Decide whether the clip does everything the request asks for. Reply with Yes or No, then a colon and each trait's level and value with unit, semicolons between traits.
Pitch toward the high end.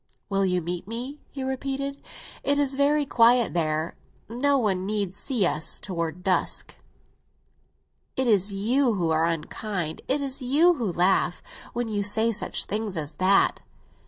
Yes: high, 210 Hz